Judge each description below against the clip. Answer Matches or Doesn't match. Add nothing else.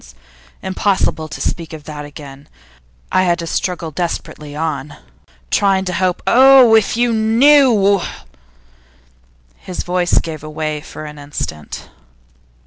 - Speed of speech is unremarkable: Doesn't match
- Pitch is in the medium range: Matches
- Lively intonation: Doesn't match